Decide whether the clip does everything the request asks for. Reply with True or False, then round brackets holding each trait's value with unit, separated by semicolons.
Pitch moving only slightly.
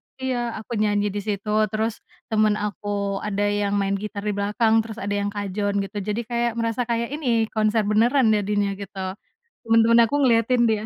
True (2.1 semitones)